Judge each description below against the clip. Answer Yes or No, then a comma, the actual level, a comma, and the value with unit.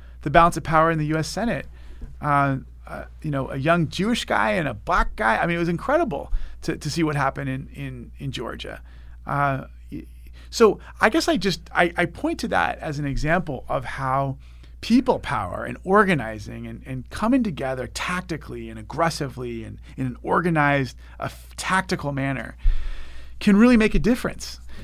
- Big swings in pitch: Yes, wide, 7.6 semitones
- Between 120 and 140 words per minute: No, average, 175 wpm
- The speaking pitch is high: No, medium, 140 Hz